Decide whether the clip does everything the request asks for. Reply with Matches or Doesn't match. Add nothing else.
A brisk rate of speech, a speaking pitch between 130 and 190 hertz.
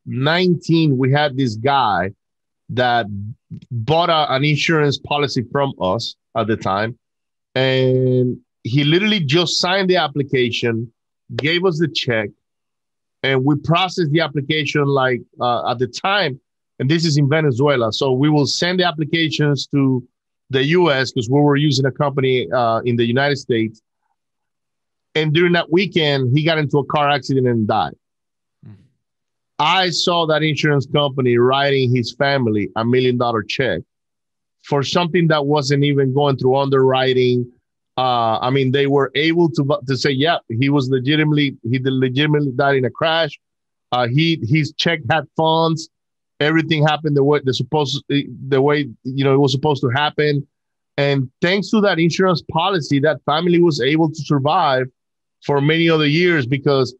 Doesn't match